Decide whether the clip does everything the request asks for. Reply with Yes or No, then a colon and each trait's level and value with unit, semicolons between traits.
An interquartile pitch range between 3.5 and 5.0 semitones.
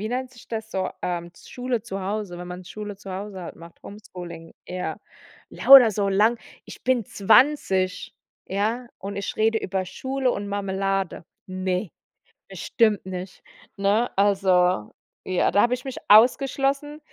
Yes: average, 4.1 semitones